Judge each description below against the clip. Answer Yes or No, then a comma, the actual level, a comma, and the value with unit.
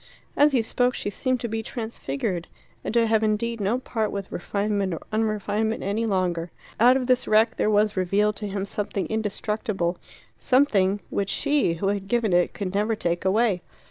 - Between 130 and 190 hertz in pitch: No, high, 210 Hz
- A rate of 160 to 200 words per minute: Yes, average, 180 wpm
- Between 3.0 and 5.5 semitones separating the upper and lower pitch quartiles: No, narrow, 2.5 semitones